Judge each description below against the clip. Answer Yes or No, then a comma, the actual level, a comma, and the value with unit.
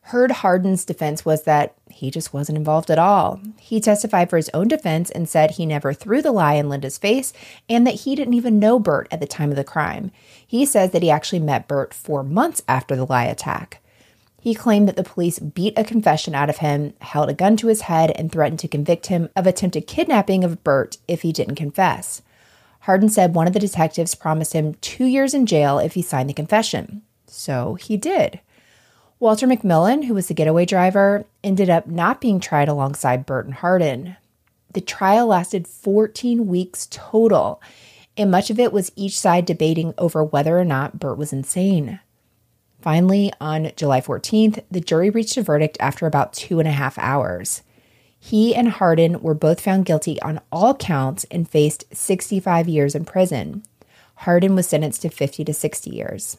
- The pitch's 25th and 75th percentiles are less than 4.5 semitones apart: No, average, 5.1 semitones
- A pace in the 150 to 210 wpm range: Yes, average, 195 wpm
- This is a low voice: No, medium, 170 Hz